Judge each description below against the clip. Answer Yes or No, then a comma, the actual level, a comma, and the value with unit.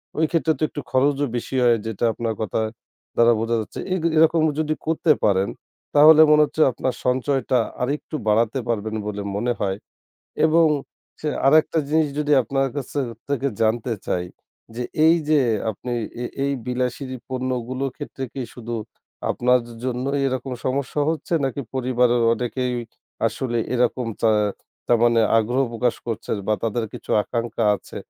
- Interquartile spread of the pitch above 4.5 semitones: No, average, 3.2 semitones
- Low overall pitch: Yes, low, 125 Hz